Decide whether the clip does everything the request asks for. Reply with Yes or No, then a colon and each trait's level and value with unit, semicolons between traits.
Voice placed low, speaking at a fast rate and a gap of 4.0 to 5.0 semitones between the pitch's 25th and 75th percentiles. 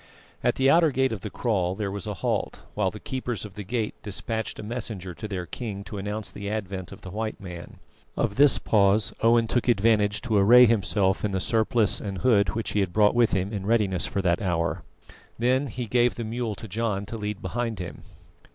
No: low, 105 Hz; fast, 215 wpm; average, 3.1 semitones